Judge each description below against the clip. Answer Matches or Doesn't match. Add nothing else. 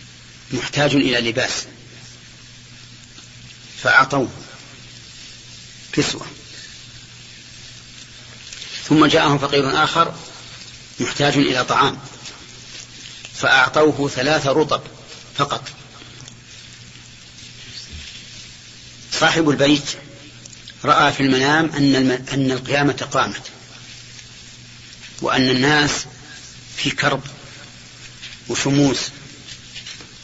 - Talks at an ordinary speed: Doesn't match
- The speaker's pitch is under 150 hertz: Matches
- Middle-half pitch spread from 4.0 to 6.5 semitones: Doesn't match